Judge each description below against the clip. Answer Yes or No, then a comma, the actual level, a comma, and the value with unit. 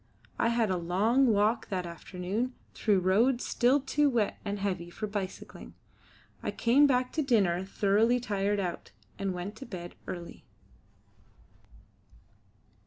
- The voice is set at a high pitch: Yes, high, 205 Hz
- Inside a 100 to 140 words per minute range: Yes, slow, 135 wpm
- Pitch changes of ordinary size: Yes, average, 4.5 semitones